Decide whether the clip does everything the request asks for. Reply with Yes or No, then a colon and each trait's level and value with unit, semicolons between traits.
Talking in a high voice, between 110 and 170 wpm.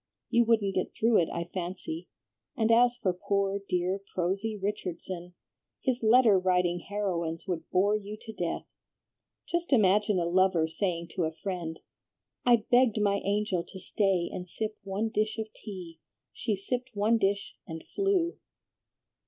Yes: high, 195 Hz; average, 155 wpm